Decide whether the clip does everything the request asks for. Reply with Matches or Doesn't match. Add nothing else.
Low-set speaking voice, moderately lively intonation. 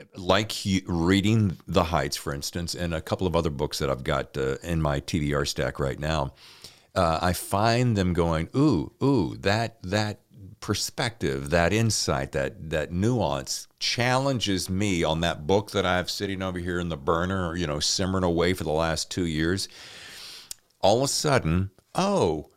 Matches